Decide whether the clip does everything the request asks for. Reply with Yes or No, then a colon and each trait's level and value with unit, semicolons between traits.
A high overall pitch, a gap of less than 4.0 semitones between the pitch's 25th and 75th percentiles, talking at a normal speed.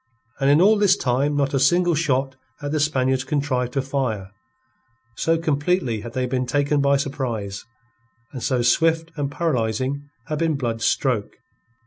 No: medium, 140 Hz; average, 3.2 semitones; average, 160 wpm